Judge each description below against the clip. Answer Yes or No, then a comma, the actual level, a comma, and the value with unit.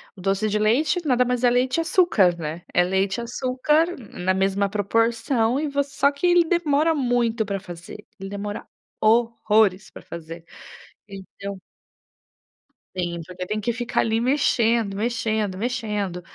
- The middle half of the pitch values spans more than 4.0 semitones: Yes, average, 4.4 semitones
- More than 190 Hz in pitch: Yes, high, 220 Hz